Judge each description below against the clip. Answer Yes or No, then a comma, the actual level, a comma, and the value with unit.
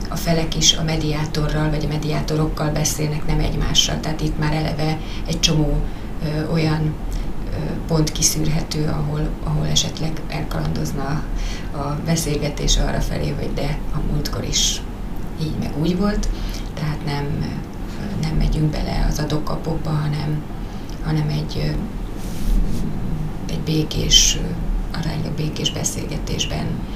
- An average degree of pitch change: No, narrow, 0.9 semitones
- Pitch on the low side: No, medium, 155 Hz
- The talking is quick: No, average, 120 wpm